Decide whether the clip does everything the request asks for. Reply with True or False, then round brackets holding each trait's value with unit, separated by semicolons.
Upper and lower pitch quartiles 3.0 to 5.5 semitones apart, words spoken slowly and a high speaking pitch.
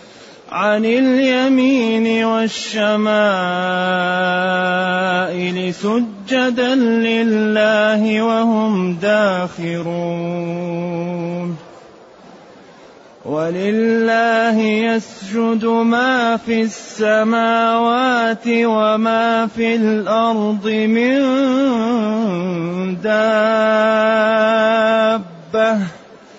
True (3.6 semitones; 40 wpm; 220 Hz)